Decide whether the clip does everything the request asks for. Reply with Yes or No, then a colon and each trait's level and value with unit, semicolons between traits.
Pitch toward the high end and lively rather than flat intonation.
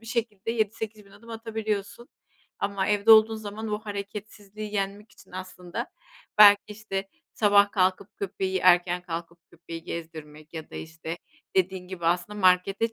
No: high, 200 Hz; average, 2.9 semitones